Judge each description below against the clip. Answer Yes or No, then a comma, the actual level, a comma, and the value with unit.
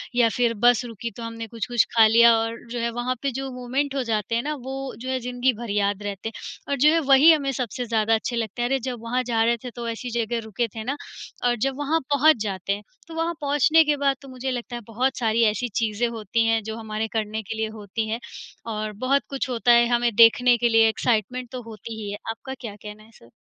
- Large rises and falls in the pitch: No, narrow, 2.4 semitones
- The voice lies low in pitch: No, high, 235 Hz